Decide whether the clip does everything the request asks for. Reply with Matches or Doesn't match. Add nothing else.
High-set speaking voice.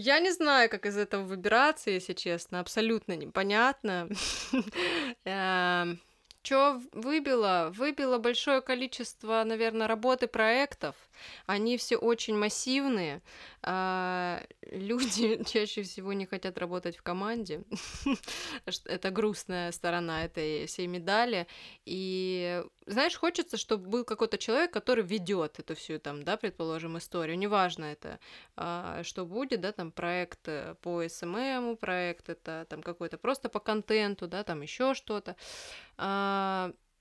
Matches